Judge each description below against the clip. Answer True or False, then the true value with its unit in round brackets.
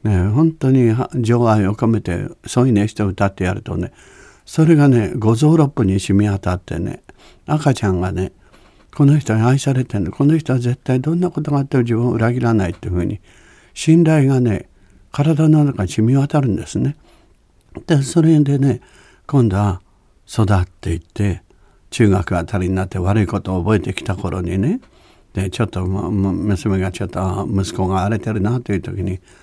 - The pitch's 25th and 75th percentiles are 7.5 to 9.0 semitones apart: False (5.5 semitones)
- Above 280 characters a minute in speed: True (330 characters per minute)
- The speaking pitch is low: True (110 Hz)